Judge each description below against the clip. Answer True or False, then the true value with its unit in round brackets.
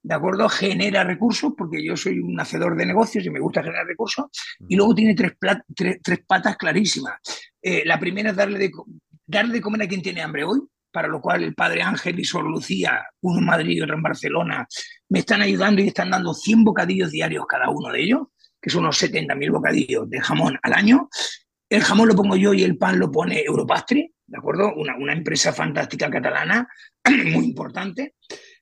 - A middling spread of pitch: False (5.7 semitones)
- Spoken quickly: True (205 wpm)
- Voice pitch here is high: True (205 Hz)